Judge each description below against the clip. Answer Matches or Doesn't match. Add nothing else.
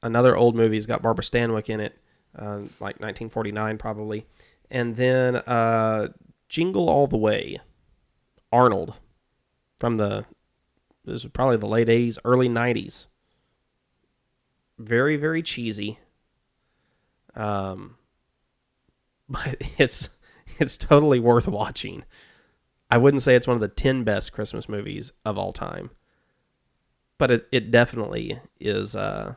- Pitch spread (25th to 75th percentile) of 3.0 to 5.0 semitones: Doesn't match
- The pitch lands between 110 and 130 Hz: Matches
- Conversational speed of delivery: Doesn't match